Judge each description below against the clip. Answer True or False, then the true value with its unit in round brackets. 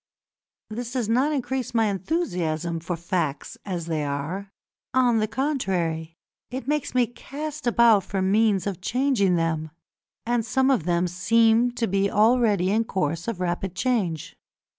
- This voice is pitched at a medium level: False (205 Hz)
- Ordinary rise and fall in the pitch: False (5.9 semitones)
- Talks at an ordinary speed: True (150 wpm)